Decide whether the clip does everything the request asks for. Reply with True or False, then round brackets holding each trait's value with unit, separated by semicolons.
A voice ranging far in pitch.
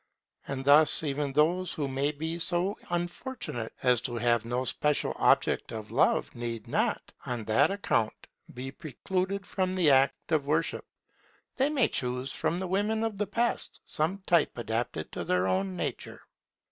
True (7.0 semitones)